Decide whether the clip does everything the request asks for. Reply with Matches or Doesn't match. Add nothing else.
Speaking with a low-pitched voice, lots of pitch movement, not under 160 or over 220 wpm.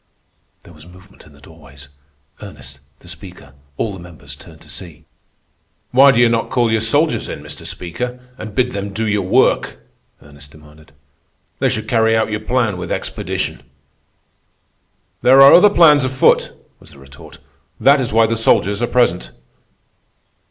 Matches